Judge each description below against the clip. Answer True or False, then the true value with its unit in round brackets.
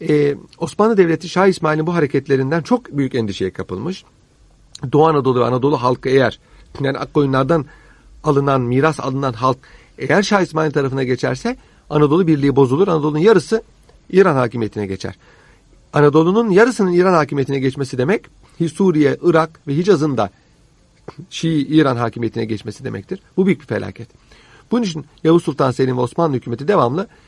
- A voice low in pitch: False (145 Hz)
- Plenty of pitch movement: False (4.4 semitones)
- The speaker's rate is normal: False (145 wpm)